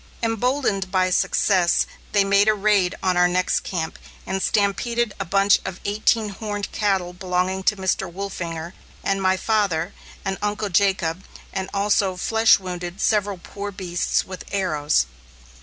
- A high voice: Yes, high, 195 Hz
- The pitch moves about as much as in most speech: No, narrow, 2.2 semitones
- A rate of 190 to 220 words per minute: No, average, 145 wpm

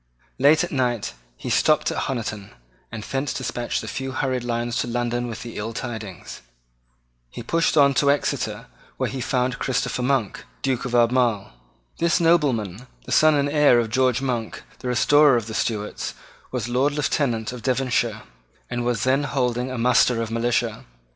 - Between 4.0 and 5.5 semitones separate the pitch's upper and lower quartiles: No, average, 2.7 semitones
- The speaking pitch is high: No, low, 125 Hz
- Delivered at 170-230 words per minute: Yes, average, 175 wpm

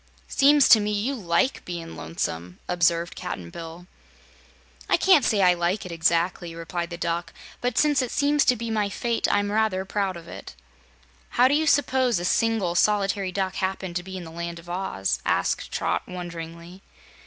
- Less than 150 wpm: No, average, 180 wpm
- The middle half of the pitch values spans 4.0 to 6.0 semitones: Yes, average, 4.5 semitones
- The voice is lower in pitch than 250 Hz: Yes, medium, 185 Hz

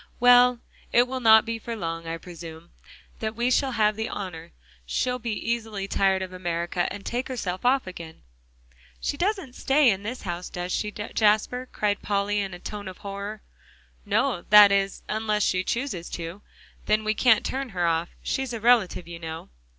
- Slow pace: No, average, 180 wpm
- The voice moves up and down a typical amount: Yes, average, 4.7 semitones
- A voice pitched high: Yes, high, 210 Hz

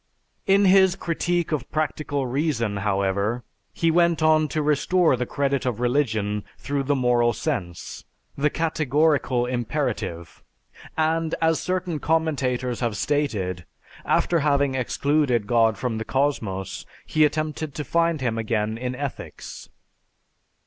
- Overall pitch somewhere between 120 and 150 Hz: Yes, medium, 140 Hz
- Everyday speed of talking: No, slow, 130 wpm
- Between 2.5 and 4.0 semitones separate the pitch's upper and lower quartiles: No, average, 5.0 semitones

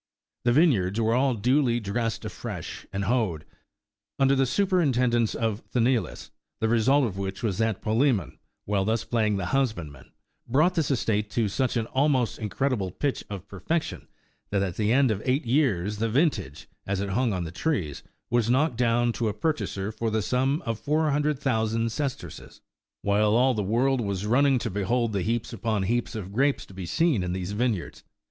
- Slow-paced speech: No, average, 180 wpm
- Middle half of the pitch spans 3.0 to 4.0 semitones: No, average, 4.5 semitones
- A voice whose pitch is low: Yes, low, 115 Hz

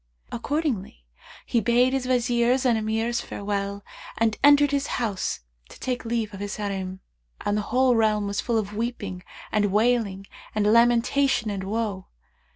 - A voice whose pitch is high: Yes, high, 225 Hz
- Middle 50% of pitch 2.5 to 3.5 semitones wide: Yes, average, 3.2 semitones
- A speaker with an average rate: Yes, average, 155 wpm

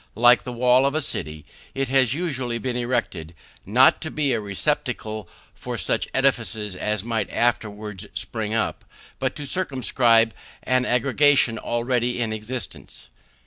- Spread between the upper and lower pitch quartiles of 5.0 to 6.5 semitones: No, average, 3.2 semitones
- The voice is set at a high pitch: No, low, 120 Hz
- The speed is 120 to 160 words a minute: Yes, average, 145 wpm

